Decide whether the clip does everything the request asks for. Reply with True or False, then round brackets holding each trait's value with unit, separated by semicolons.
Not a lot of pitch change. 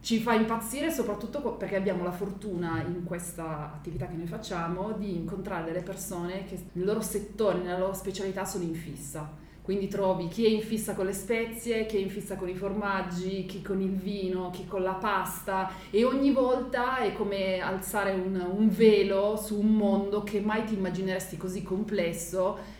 True (2.2 semitones)